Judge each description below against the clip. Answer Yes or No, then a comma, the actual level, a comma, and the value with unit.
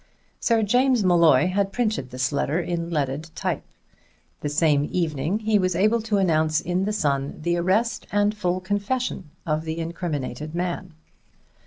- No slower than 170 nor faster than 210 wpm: No, average, 155 wpm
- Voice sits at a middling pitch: Yes, medium, 175 Hz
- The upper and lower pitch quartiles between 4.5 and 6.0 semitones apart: Yes, average, 4.8 semitones